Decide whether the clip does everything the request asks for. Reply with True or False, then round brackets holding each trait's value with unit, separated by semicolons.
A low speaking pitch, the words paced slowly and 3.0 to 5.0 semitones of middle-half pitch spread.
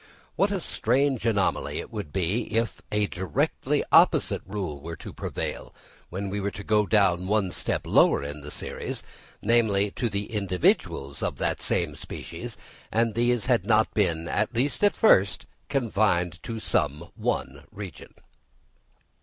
False (100 Hz; 145 wpm; 4.7 semitones)